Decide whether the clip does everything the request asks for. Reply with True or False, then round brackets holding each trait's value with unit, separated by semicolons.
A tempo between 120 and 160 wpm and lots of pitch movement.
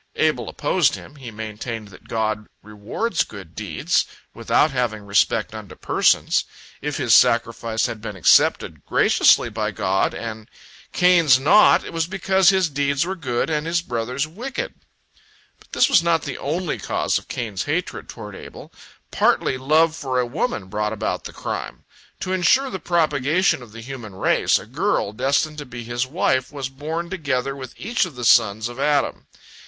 False (170 wpm; 6.4 semitones)